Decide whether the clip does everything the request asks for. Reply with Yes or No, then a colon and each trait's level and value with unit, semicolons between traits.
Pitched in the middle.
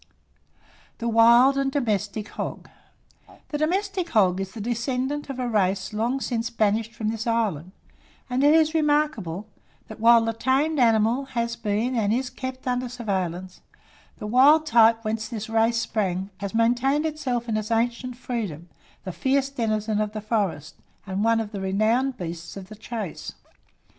No: high, 230 Hz